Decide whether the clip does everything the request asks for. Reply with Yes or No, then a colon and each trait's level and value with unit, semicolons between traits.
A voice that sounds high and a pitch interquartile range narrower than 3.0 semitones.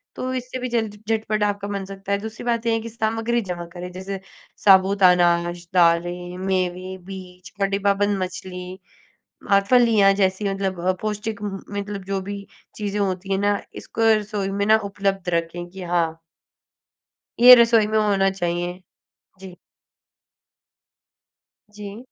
Yes: high, 195 Hz; narrow, 2.5 semitones